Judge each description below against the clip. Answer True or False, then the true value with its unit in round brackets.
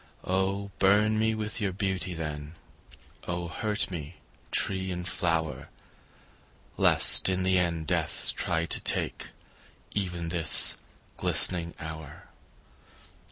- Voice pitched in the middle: False (90 Hz)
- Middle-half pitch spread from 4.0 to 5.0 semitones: False (2.7 semitones)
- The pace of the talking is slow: True (115 wpm)